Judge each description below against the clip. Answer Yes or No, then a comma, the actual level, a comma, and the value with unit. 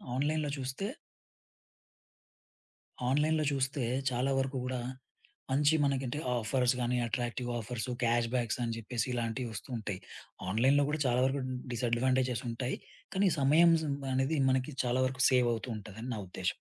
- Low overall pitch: Yes, low, 130 Hz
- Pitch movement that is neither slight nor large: No, narrow, 2.3 semitones